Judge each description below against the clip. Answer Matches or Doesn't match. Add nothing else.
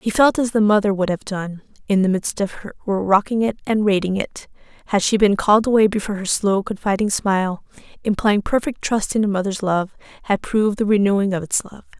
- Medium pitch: Doesn't match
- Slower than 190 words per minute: Doesn't match